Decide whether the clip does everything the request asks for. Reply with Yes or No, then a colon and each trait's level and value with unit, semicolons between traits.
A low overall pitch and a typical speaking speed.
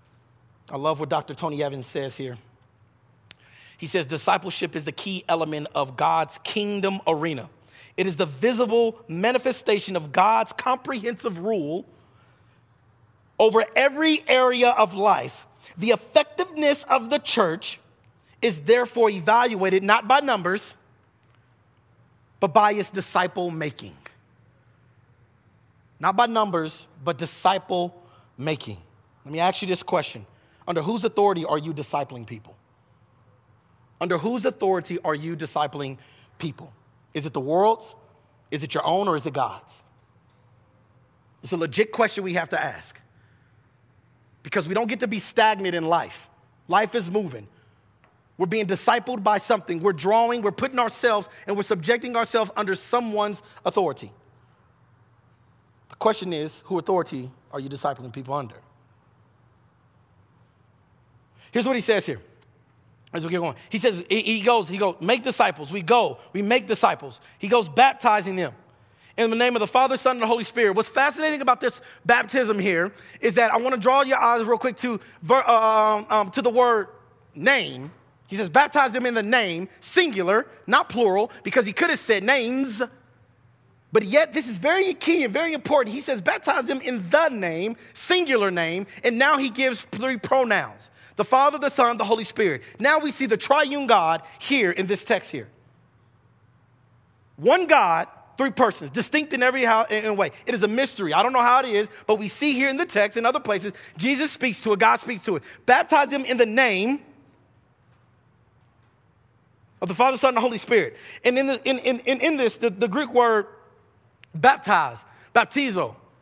No: high, 195 Hz; average, 165 wpm